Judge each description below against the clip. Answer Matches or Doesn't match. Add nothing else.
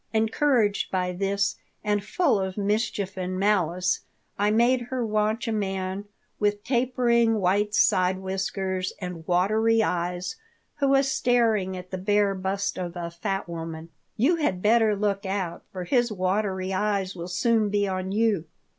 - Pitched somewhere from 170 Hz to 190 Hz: Doesn't match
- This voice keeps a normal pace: Matches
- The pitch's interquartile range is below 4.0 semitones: Matches